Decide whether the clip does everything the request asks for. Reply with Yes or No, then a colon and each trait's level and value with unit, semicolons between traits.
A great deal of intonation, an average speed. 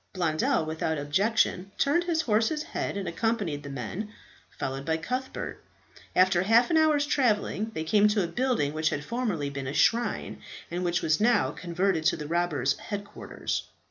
Yes: wide, 6.4 semitones; average, 170 wpm